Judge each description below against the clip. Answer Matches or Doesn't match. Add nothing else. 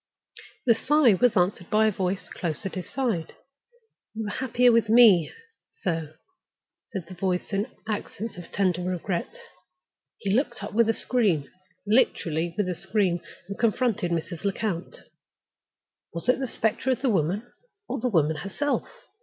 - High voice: Matches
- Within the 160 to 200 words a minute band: Doesn't match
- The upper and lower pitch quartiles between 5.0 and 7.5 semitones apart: Doesn't match